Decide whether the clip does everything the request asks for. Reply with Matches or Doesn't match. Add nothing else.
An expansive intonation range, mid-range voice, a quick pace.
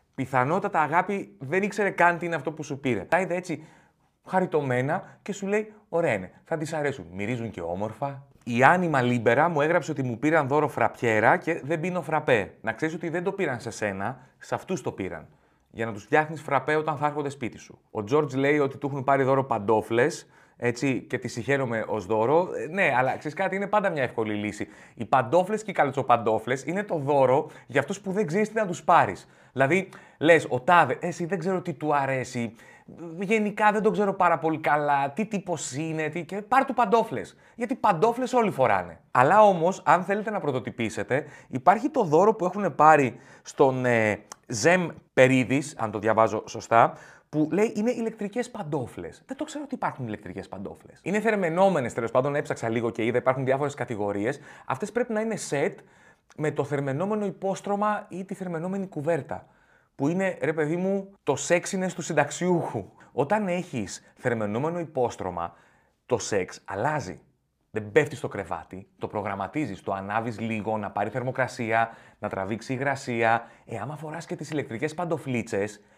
Matches